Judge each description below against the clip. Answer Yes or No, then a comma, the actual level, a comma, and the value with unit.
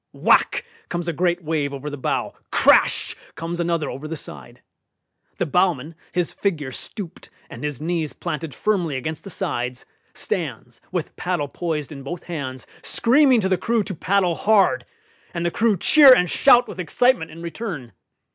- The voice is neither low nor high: Yes, medium, 170 Hz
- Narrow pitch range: No, average, 4.5 semitones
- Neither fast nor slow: Yes, average, 165 wpm